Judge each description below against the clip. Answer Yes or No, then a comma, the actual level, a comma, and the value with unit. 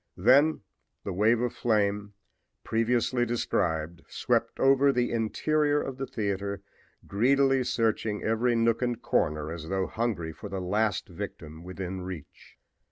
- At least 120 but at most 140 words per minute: Yes, slow, 135 wpm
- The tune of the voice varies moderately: Yes, average, 4.5 semitones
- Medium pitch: No, low, 110 Hz